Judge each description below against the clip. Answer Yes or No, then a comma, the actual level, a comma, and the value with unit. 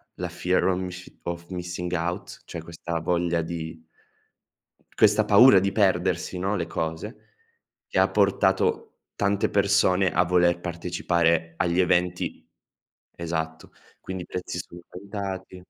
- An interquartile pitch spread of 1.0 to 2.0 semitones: Yes, narrow, 1.6 semitones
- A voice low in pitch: Yes, very low, 90 Hz